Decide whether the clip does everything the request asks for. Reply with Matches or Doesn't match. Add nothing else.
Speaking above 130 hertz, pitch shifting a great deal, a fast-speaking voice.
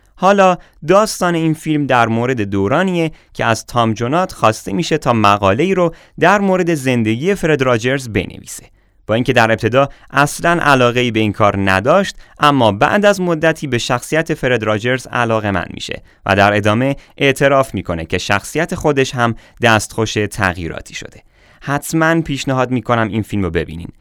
Doesn't match